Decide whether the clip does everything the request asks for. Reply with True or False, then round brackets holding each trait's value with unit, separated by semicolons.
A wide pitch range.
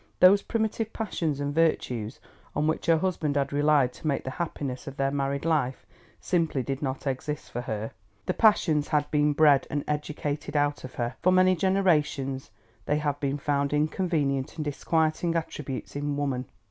False (2.8 semitones)